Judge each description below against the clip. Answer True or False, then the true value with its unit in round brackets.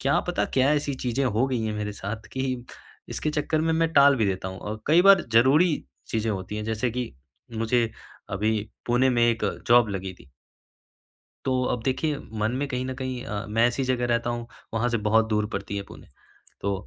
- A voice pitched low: True (120 Hz)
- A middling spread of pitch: True (3.6 semitones)